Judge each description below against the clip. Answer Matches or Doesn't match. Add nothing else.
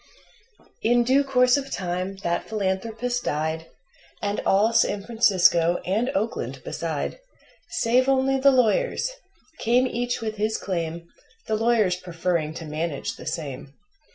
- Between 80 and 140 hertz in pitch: Doesn't match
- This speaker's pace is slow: Matches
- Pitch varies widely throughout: Matches